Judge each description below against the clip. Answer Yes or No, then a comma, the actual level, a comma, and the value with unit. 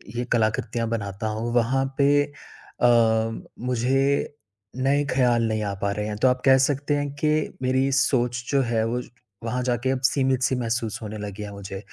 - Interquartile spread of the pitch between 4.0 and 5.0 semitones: No, average, 3.2 semitones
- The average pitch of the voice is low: Yes, low, 120 Hz